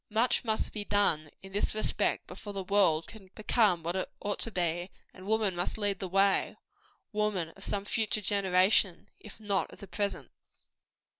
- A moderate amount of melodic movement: No, narrow, 2.3 semitones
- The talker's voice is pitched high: Yes, high, 200 Hz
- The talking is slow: No, average, 175 wpm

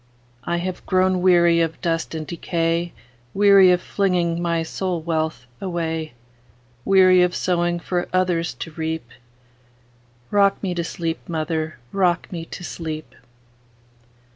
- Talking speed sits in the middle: No, slow, 115 wpm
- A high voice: No, medium, 165 Hz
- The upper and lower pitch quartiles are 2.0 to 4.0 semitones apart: Yes, narrow, 2.5 semitones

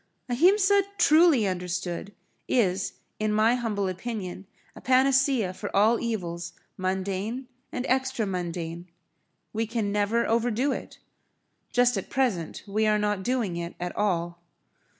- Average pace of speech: No, slow, 130 wpm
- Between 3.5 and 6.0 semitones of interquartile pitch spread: Yes, average, 4.9 semitones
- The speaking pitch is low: No, high, 210 Hz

